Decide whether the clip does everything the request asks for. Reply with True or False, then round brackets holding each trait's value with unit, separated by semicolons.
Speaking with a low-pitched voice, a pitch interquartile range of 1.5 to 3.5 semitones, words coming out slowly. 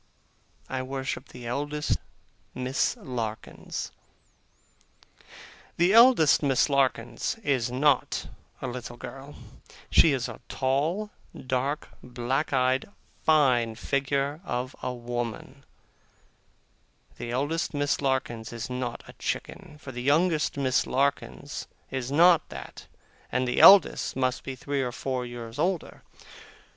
True (130 Hz; 2.6 semitones; 120 wpm)